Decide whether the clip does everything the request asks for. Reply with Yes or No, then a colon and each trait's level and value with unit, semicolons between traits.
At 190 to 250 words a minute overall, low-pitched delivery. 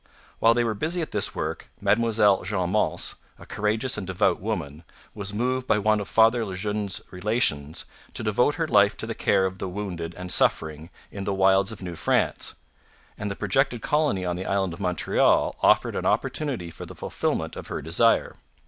Yes: average, 195 wpm; low, 100 Hz